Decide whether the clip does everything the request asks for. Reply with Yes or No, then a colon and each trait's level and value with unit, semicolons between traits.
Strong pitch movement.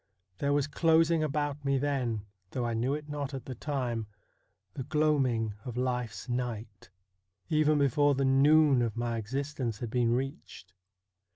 No: average, 3.6 semitones